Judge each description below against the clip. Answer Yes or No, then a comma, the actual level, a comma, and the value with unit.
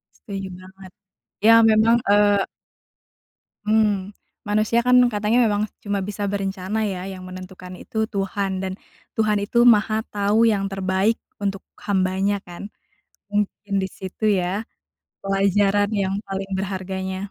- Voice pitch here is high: Yes, high, 200 Hz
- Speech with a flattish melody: Yes, narrow, 1.6 semitones